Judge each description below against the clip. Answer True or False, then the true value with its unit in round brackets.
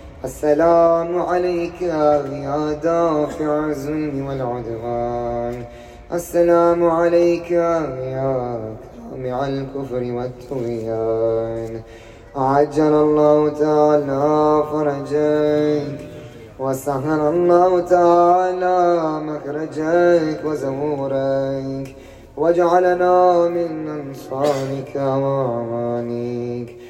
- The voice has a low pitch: False (150 Hz)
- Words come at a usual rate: False (55 wpm)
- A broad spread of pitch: False (4.4 semitones)